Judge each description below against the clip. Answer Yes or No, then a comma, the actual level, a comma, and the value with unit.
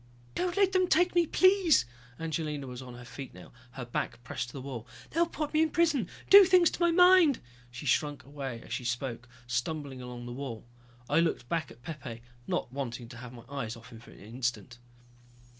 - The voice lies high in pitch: No, low, 135 Hz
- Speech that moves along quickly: Yes, fast, 210 wpm